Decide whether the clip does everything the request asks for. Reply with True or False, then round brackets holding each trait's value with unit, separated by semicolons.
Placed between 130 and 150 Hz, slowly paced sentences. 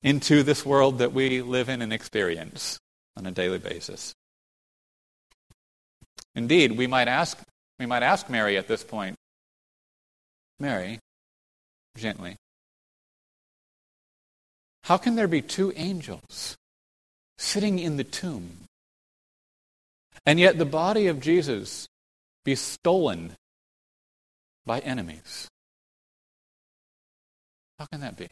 True (135 Hz; 105 wpm)